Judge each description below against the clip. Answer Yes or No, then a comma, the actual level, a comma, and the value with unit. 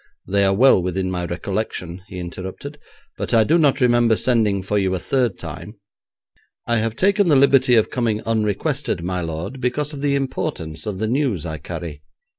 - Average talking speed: Yes, average, 185 wpm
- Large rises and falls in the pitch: Yes, wide, 6.4 semitones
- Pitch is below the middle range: Yes, low, 110 Hz